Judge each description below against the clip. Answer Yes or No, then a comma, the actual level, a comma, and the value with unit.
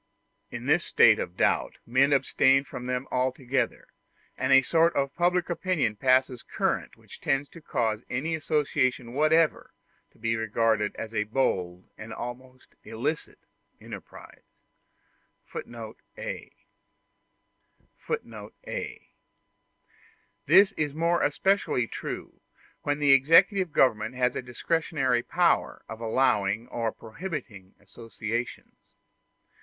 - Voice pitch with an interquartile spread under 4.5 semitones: No, average, 5.1 semitones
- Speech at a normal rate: No, slow, 115 wpm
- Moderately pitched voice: No, low, 130 Hz